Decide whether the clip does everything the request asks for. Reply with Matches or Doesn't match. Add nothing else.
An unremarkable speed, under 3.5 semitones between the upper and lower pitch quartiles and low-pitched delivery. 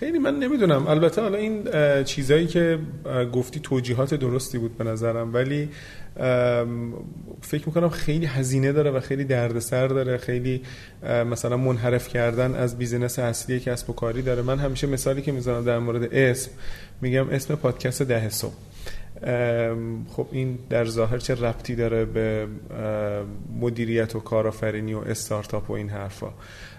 Matches